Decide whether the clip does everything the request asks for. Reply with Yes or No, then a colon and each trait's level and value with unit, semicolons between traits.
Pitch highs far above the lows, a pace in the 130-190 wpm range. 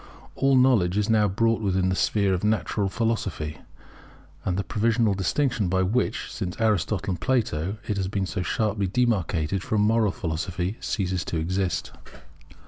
No: average, 3.2 semitones; average, 155 wpm